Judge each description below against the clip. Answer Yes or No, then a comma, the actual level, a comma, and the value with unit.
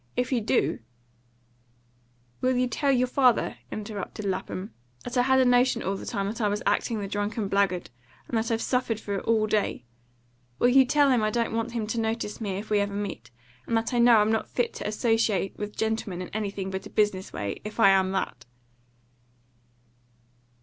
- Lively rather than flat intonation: No, average, 3.2 semitones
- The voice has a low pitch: No, high, 215 Hz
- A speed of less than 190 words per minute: No, fast, 205 wpm